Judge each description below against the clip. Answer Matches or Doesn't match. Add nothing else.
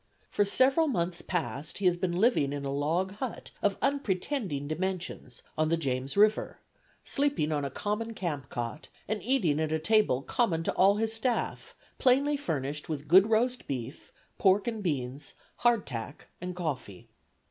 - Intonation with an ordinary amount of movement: Doesn't match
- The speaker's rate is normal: Matches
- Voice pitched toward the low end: Doesn't match